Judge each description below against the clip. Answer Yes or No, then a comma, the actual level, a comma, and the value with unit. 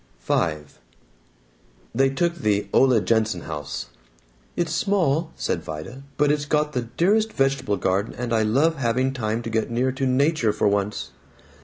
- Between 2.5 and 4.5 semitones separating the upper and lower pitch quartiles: No, average, 5.3 semitones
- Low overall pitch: Yes, low, 130 Hz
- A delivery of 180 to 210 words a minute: No, average, 155 wpm